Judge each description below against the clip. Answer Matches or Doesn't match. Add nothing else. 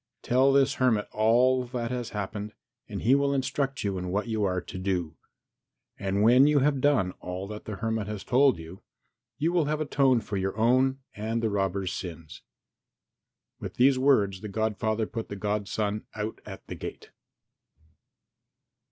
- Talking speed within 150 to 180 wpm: Matches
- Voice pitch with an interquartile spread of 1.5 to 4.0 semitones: Doesn't match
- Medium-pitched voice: Doesn't match